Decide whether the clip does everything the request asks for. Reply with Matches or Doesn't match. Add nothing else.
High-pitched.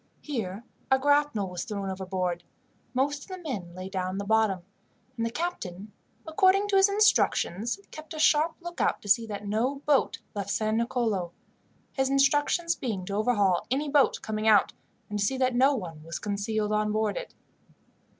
Matches